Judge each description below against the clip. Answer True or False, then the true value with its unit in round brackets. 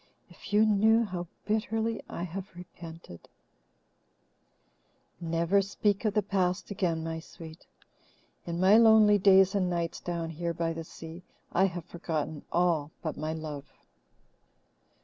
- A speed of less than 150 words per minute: True (140 wpm)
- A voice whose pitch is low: False (175 Hz)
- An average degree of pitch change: True (3.6 semitones)